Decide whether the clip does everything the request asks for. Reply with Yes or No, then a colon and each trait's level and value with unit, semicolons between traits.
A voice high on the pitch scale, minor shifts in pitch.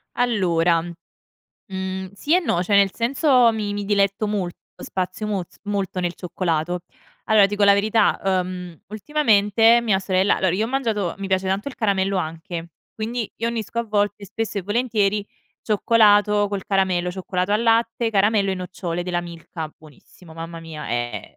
No: high, 200 Hz; average, 3.1 semitones